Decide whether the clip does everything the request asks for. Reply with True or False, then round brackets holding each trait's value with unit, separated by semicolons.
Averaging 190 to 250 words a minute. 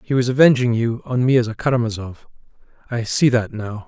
True (200 wpm)